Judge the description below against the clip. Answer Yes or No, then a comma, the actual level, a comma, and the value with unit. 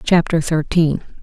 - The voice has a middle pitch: Yes, medium, 160 Hz